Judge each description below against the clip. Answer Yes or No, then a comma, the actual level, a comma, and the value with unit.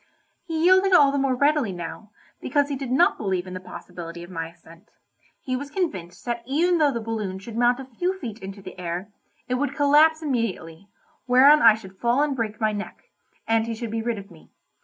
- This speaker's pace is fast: Yes, fast, 215 wpm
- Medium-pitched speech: No, high, 235 Hz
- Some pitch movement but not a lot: No, wide, 6.7 semitones